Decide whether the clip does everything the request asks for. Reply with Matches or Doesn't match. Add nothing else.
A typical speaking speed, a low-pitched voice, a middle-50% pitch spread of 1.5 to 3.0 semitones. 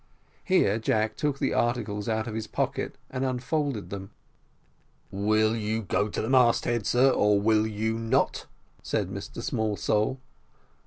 Matches